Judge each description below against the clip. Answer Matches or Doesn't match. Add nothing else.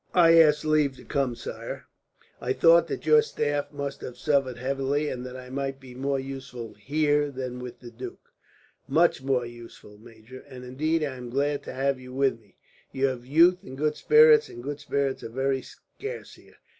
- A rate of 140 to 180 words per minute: Doesn't match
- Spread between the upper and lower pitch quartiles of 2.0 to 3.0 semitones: Matches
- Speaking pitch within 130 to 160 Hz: Matches